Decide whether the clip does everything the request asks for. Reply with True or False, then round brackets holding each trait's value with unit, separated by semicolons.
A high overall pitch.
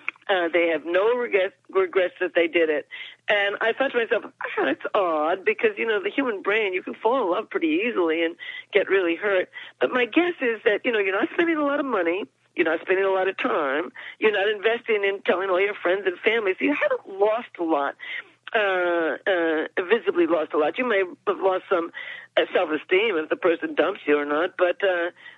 True (210 Hz)